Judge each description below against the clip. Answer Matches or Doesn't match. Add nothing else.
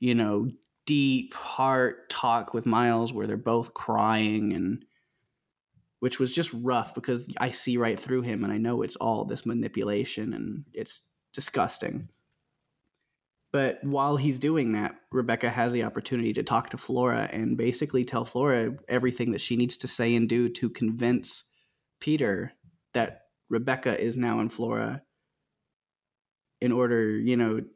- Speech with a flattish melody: Matches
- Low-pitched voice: Matches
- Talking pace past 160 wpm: Doesn't match